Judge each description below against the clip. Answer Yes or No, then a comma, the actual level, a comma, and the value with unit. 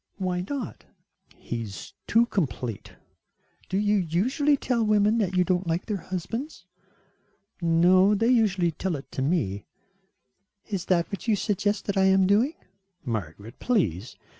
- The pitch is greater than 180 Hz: Yes, high, 190 Hz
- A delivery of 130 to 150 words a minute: Yes, average, 145 wpm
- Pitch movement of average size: Yes, average, 4.1 semitones